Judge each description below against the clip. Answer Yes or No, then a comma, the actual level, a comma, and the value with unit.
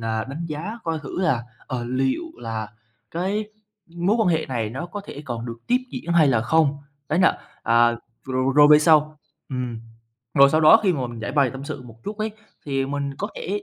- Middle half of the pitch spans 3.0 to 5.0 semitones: No, wide, 5.4 semitones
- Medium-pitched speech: Yes, medium, 145 Hz